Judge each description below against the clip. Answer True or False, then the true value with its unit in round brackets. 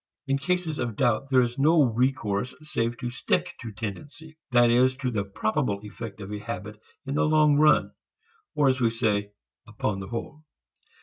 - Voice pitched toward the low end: True (120 Hz)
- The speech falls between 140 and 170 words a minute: False (180 wpm)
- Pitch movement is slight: False (4.6 semitones)